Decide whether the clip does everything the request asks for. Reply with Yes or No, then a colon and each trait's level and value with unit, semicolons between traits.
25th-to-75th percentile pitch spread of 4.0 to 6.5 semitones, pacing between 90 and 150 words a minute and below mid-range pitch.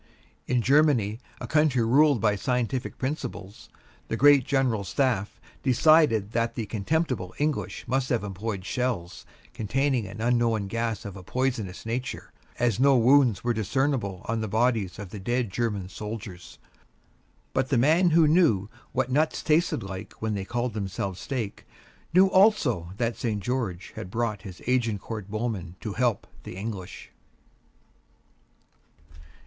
Yes: average, 4.5 semitones; average, 145 wpm; low, 115 Hz